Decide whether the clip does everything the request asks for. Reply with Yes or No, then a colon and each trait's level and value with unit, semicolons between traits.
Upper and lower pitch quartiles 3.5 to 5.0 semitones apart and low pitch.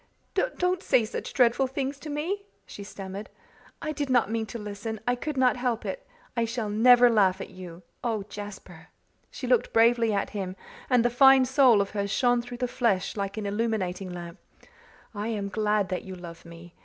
No: average, 3.9 semitones; high, 225 Hz